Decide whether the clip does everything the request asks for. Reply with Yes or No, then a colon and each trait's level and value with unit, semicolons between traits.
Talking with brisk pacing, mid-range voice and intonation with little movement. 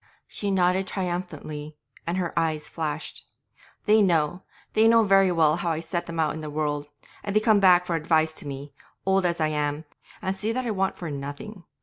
No: fast, 210 wpm; medium, 170 Hz; average, 3.8 semitones